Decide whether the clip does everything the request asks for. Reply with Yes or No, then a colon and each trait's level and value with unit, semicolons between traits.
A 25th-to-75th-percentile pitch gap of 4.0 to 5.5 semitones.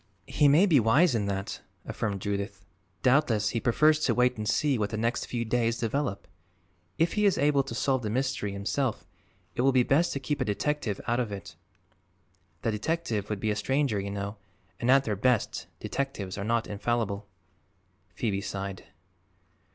Yes: average, 5.1 semitones